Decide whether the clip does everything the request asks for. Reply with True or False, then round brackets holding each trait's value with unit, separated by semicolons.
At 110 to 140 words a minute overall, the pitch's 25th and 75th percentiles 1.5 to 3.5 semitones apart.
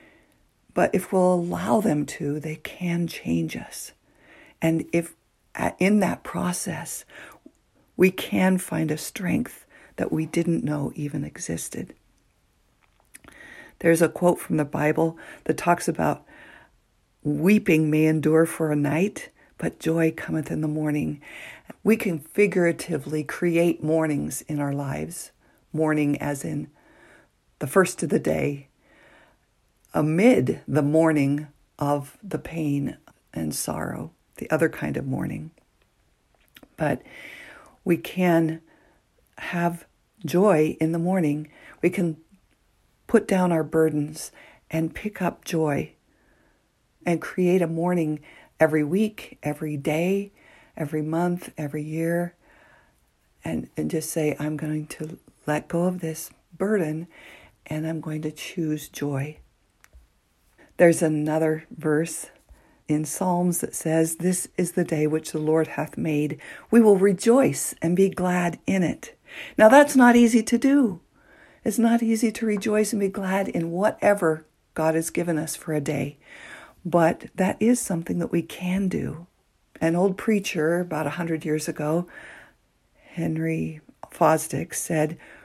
True (135 wpm; 3.0 semitones)